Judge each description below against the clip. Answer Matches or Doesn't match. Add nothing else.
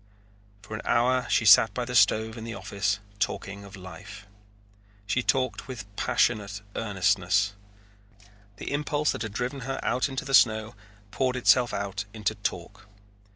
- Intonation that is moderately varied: Matches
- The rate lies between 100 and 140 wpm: Doesn't match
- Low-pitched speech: Matches